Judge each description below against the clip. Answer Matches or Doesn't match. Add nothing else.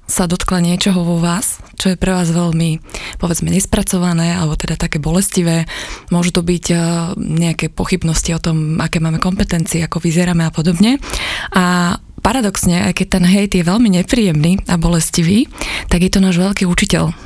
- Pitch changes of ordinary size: Doesn't match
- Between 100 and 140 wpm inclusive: Doesn't match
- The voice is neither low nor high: Matches